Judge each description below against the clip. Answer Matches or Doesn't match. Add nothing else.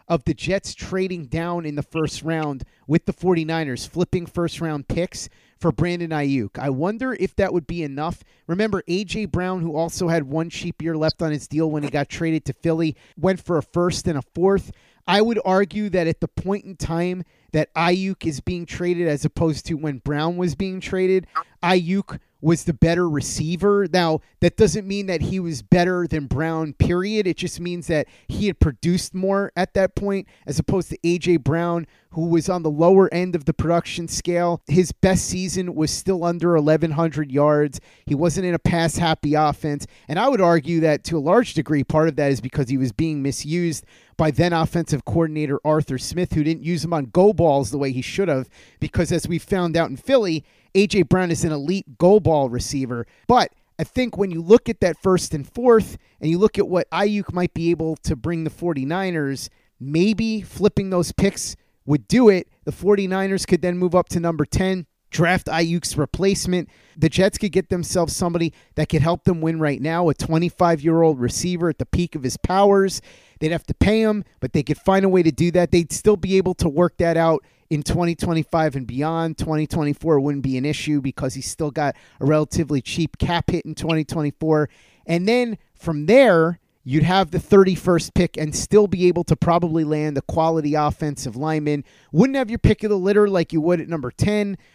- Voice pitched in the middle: Matches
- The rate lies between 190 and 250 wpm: Matches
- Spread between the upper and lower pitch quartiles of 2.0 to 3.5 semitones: Matches